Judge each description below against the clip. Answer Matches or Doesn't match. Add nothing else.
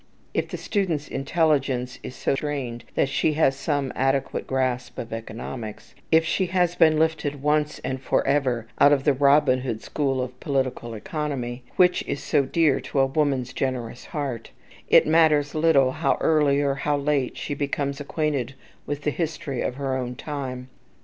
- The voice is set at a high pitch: Doesn't match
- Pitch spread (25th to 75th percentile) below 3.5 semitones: Matches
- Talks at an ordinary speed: Matches